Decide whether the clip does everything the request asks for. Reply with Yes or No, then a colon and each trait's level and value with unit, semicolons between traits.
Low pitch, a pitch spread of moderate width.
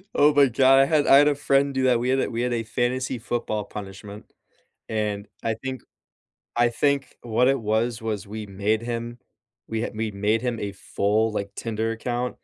Yes: low, 115 Hz; average, 3.2 semitones